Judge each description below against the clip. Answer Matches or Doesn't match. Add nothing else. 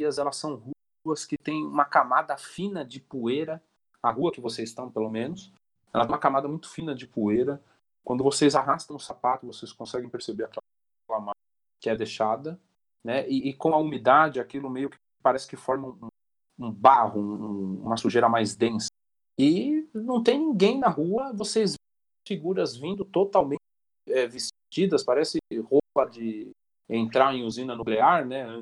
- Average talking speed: Matches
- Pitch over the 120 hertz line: Matches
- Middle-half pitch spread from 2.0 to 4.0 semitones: Doesn't match